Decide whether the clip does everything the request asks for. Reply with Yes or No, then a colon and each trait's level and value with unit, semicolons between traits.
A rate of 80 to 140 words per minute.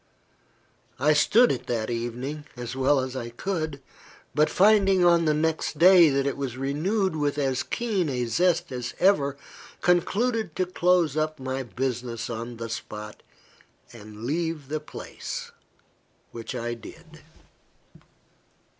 Yes: slow, 135 wpm